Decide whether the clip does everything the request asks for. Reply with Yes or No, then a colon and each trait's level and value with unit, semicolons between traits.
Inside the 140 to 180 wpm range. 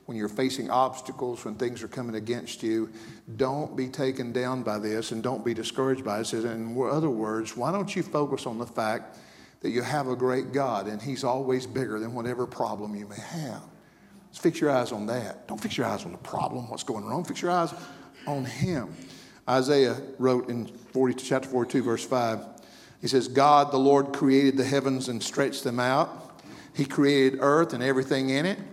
No: fast, 205 wpm